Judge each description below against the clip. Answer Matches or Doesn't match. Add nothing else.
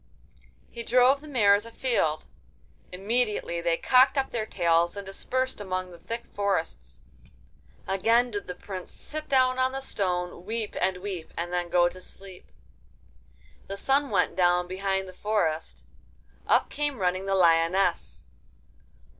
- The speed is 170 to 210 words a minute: Doesn't match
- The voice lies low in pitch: Doesn't match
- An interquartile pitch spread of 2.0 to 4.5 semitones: Doesn't match